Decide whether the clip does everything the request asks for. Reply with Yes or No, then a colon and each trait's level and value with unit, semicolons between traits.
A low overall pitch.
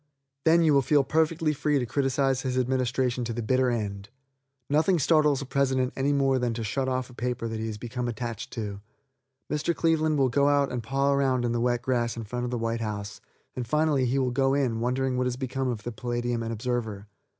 Yes: low, 125 Hz